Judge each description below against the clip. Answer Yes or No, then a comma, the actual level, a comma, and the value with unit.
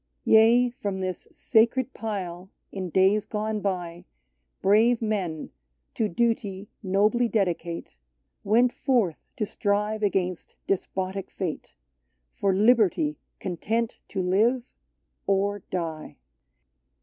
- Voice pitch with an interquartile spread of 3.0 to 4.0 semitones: Yes, average, 3.3 semitones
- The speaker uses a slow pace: Yes, slow, 115 wpm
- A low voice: No, high, 200 Hz